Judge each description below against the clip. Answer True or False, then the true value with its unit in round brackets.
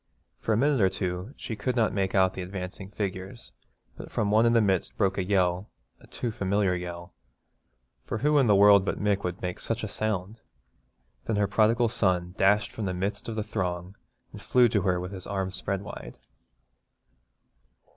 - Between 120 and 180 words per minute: False (195 wpm)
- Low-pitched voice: True (100 Hz)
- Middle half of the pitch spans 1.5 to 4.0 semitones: True (2.8 semitones)